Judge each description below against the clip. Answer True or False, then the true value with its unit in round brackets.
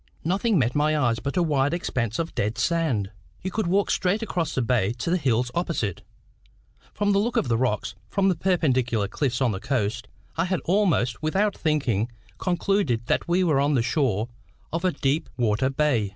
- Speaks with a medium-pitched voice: True (145 Hz)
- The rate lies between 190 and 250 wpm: True (195 wpm)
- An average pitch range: False (6.8 semitones)